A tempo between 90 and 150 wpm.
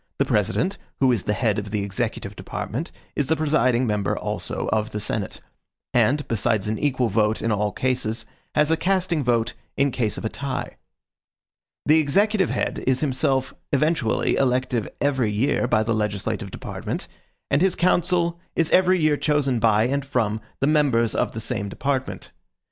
No: average, 170 wpm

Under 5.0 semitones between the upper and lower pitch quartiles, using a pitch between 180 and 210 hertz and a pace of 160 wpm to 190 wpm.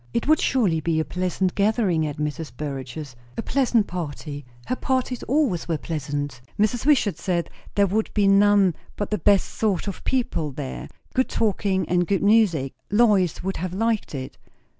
No: wide, 5.5 semitones; high, 190 Hz; average, 170 wpm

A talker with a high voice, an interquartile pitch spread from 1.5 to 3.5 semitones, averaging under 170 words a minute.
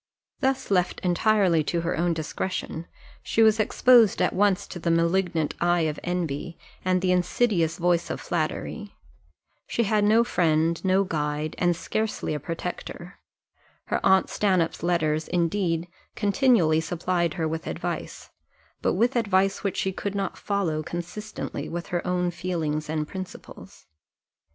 No: medium, 175 Hz; average, 3.1 semitones; average, 145 wpm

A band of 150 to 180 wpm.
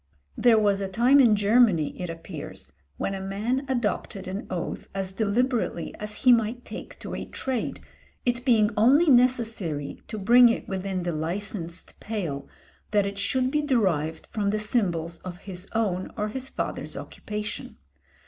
Yes: average, 160 wpm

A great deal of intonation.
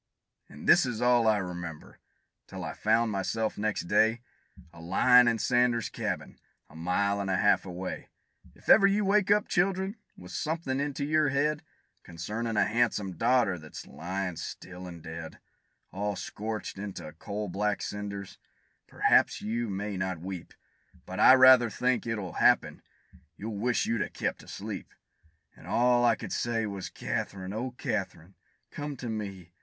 No: average, 4.6 semitones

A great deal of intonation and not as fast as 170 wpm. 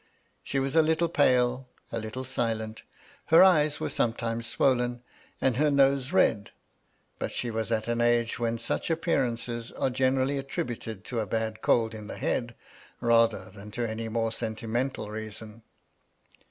No: average, 2.8 semitones; average, 155 wpm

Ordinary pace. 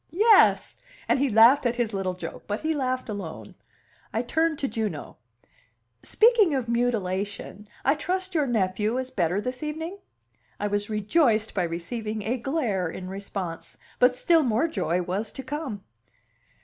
Yes: average, 155 wpm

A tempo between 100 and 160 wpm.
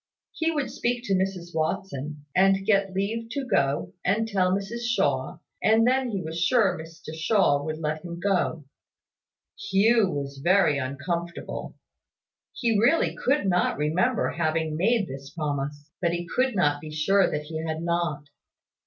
Yes: average, 155 wpm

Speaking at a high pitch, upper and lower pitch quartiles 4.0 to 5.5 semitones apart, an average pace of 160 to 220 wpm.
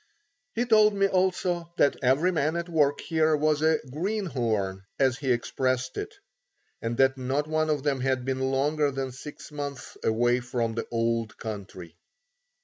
No: low, 135 Hz; average, 4.3 semitones; average, 165 wpm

